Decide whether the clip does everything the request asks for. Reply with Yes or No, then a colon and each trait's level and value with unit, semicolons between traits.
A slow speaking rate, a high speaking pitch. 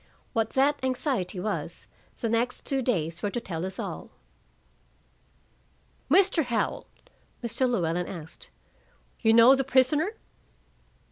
Yes: slow, 120 wpm; high, 235 Hz